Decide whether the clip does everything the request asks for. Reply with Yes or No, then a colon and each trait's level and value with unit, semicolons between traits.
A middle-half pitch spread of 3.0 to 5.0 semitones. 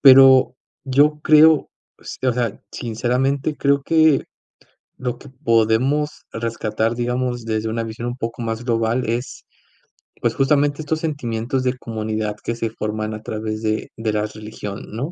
Yes: average, 3.4 semitones